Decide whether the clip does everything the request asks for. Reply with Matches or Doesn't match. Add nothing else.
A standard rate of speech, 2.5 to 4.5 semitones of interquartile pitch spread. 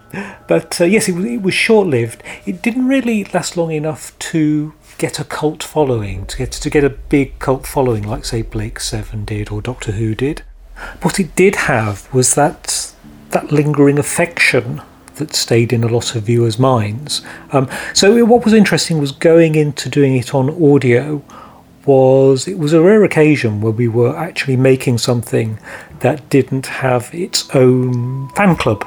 Doesn't match